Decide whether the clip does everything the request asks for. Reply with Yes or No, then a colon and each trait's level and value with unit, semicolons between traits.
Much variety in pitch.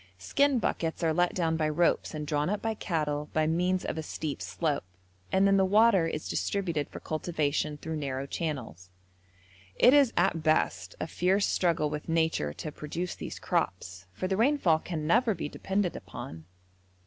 No: average, 4.0 semitones